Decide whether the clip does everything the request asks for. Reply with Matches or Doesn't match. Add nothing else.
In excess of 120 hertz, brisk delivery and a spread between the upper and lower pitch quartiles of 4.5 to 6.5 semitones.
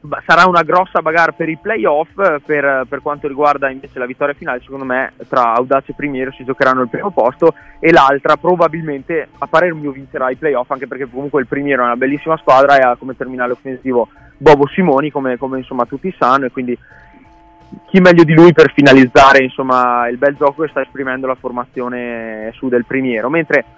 Doesn't match